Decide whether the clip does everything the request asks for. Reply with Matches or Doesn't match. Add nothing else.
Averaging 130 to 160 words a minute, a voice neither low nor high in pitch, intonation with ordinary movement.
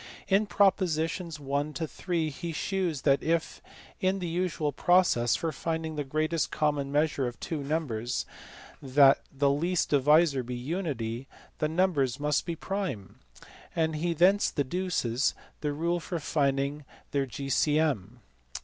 Matches